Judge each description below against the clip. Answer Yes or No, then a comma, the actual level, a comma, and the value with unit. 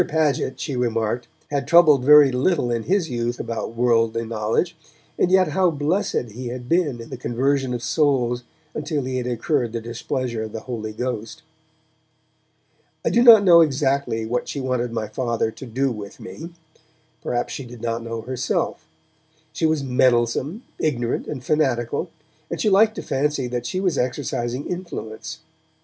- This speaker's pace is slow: No, average, 165 wpm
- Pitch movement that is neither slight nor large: Yes, average, 4.1 semitones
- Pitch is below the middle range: Yes, low, 125 Hz